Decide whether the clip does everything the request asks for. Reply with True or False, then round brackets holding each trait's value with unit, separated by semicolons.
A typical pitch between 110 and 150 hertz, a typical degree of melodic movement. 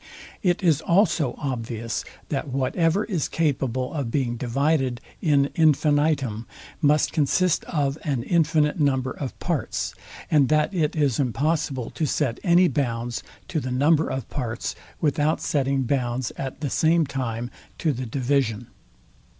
True (140 Hz; 3.6 semitones)